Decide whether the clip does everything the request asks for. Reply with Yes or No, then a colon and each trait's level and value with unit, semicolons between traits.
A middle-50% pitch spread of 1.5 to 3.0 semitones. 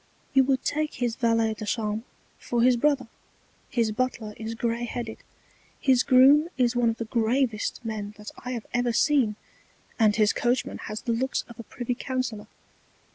Yes: narrow, 2.4 semitones